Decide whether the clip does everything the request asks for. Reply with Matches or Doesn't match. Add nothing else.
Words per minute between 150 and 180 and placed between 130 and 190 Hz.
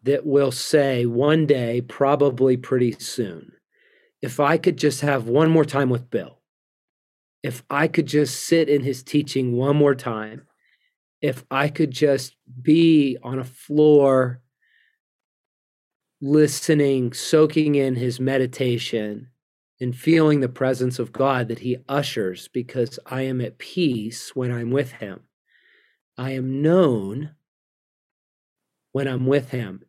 Doesn't match